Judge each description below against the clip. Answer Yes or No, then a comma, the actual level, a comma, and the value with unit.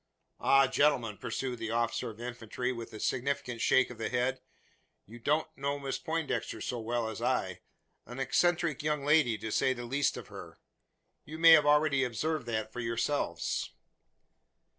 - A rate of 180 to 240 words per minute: No, average, 165 wpm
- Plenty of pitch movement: No, average, 4.0 semitones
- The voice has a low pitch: Yes, low, 125 Hz